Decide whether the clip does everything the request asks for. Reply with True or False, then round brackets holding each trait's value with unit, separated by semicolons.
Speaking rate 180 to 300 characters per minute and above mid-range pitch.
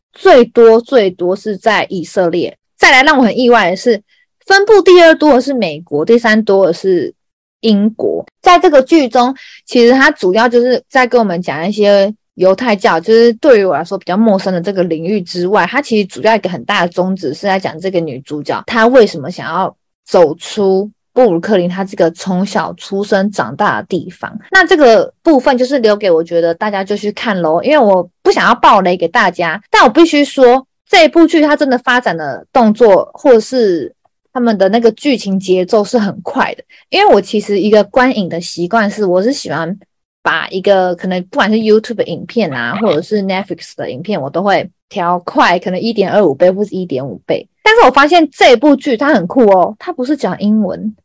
False (310 characters per minute; 215 Hz)